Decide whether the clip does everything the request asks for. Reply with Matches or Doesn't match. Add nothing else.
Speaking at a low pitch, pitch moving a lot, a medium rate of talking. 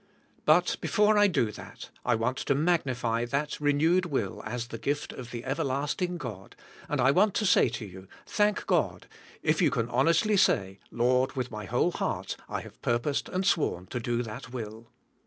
Matches